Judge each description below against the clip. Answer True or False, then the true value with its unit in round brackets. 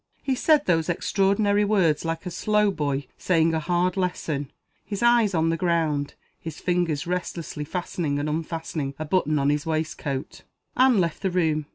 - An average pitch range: True (3.6 semitones)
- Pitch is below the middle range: False (165 Hz)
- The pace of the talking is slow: False (170 wpm)